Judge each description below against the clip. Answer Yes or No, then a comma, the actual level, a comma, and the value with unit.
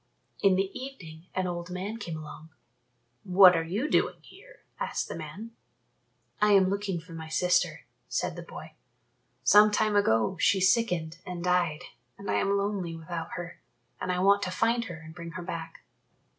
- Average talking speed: Yes, average, 175 wpm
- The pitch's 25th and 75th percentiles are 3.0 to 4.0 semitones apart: Yes, average, 3.3 semitones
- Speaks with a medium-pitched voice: Yes, medium, 180 Hz